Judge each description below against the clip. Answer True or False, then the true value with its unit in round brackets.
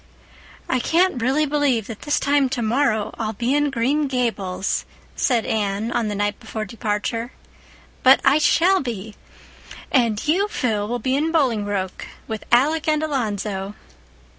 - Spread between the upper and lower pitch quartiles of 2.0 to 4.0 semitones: False (5.1 semitones)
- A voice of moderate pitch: False (240 Hz)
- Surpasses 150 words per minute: False (145 wpm)